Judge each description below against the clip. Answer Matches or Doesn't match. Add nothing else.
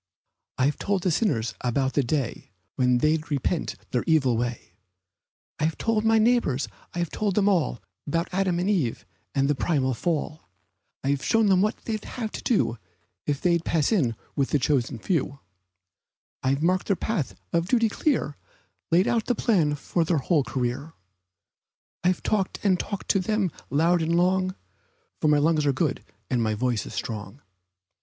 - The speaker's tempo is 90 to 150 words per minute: Doesn't match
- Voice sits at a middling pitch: Matches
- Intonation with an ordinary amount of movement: Doesn't match